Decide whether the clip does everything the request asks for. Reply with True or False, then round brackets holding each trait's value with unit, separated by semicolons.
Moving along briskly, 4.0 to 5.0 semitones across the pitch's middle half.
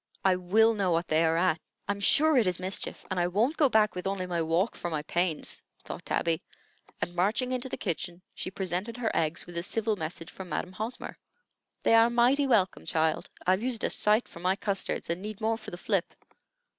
True (215 wpm; 4.3 semitones)